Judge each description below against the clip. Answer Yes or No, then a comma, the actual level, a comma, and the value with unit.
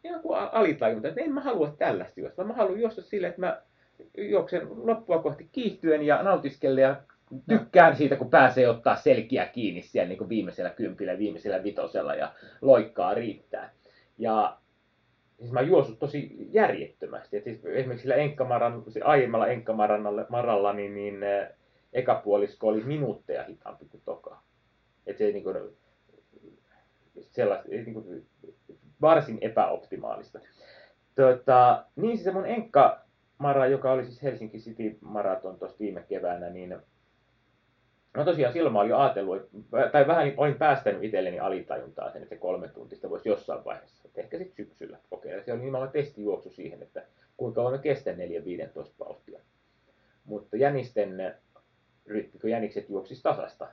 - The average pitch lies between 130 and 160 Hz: Yes, medium, 140 Hz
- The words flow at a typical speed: Yes, average, 140 wpm